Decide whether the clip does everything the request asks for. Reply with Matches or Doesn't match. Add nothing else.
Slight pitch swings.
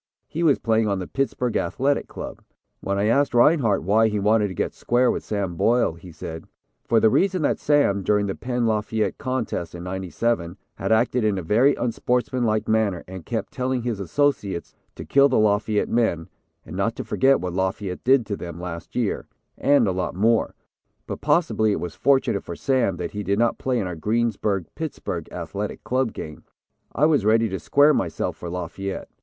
Doesn't match